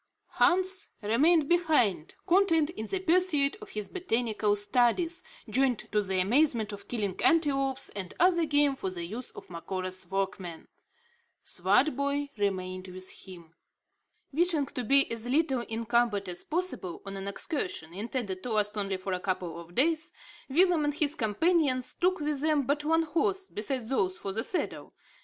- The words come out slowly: No, average, 155 wpm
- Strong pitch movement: Yes, wide, 8.1 semitones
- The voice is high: Yes, high, 245 Hz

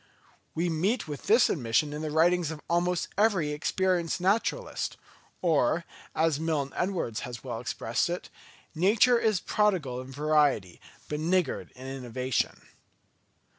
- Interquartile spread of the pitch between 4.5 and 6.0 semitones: Yes, average, 5.1 semitones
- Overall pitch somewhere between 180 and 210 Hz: No, medium, 160 Hz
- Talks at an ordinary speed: No, slow, 130 wpm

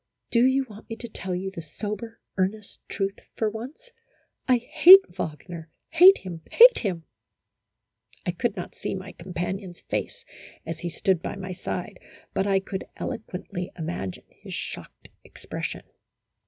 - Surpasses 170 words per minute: No, average, 155 wpm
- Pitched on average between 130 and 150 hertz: No, high, 195 Hz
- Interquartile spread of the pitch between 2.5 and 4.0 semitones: No, average, 4.4 semitones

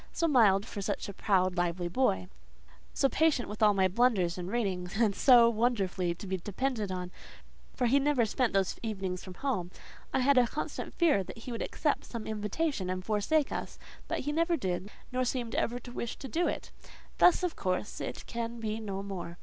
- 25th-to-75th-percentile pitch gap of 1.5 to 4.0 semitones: No, average, 5.1 semitones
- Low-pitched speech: No, high, 215 Hz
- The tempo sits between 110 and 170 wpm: No, average, 200 wpm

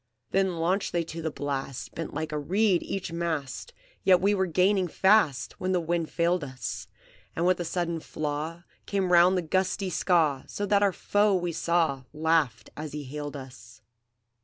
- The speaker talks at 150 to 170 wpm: No, average, 180 wpm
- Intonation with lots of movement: No, average, 3.8 semitones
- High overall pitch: No, medium, 170 Hz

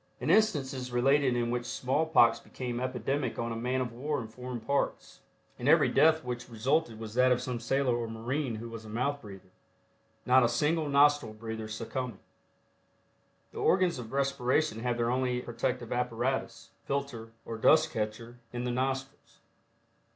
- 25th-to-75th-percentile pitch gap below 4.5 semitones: Yes, average, 2.8 semitones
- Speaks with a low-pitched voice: Yes, low, 125 Hz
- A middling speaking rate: Yes, average, 170 wpm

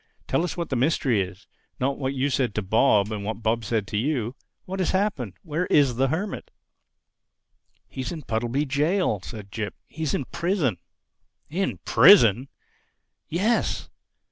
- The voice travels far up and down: Yes, wide, 6.4 semitones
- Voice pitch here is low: Yes, low, 130 Hz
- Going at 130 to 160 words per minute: Yes, average, 150 wpm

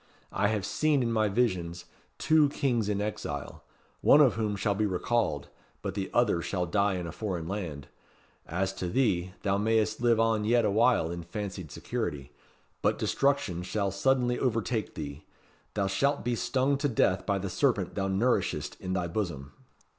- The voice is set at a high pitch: No, low, 105 Hz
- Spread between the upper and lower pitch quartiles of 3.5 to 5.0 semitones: Yes, average, 4.7 semitones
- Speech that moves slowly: No, average, 170 wpm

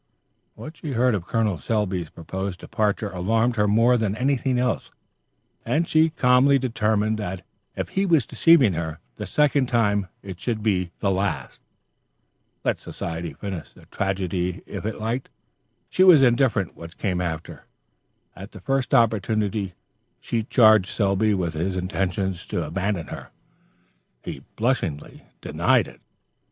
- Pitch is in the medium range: No, low, 105 Hz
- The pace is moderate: Yes, average, 145 wpm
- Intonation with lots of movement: No, average, 4.8 semitones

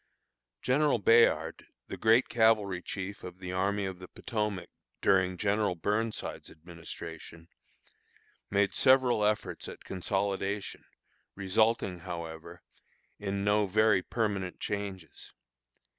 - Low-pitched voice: Yes, low, 100 Hz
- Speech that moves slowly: Yes, slow, 105 wpm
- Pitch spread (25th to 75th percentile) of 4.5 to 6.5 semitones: No, average, 2.7 semitones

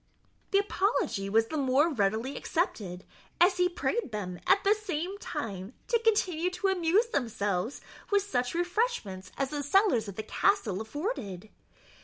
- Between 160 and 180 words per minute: No, average, 150 wpm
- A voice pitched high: Yes, very high, 290 Hz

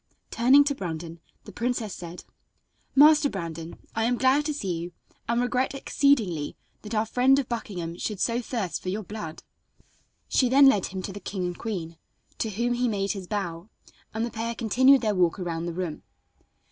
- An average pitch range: No, wide, 5.7 semitones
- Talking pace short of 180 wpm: No, average, 185 wpm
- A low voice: No, high, 215 Hz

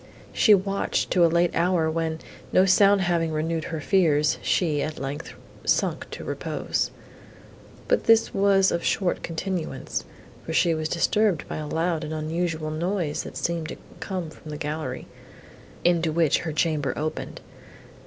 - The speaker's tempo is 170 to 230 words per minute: No, average, 155 wpm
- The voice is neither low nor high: Yes, medium, 165 Hz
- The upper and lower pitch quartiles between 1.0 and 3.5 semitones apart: Yes, average, 2.7 semitones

